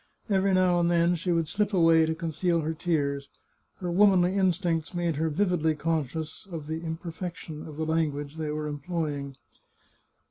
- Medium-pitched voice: Yes, medium, 165 Hz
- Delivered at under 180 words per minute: Yes, average, 170 wpm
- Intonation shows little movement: Yes, narrow, 2.3 semitones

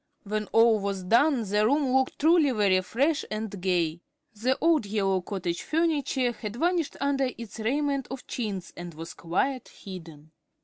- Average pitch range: No, wide, 6.3 semitones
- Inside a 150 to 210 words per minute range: Yes, average, 160 wpm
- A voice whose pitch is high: Yes, high, 220 Hz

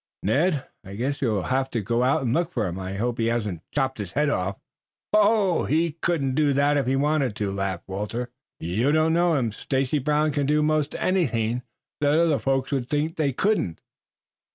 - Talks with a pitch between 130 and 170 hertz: Yes, low, 135 Hz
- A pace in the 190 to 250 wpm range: Yes, average, 195 wpm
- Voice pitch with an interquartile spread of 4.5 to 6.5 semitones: Yes, average, 5.1 semitones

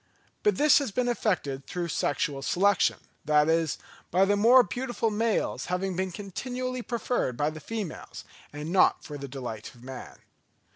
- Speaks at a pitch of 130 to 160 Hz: No, medium, 185 Hz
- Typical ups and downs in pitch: No, wide, 7.6 semitones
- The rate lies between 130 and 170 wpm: Yes, average, 160 wpm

